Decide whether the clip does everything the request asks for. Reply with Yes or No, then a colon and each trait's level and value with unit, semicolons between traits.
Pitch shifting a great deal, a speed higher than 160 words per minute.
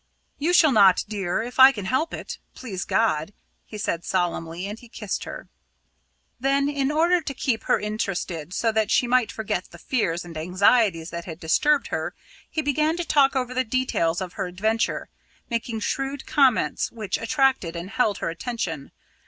Yes: wide, 6.7 semitones; average, 175 wpm